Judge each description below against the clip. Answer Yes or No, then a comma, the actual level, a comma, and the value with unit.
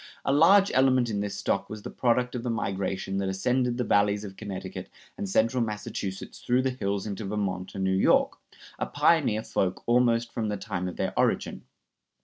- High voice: No, low, 105 Hz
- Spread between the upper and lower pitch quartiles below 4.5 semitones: Yes, average, 4.1 semitones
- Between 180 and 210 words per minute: Yes, average, 190 wpm